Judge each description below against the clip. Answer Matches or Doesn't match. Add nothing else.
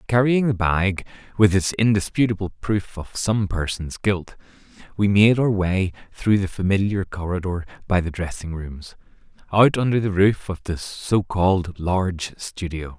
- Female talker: Doesn't match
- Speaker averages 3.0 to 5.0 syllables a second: Matches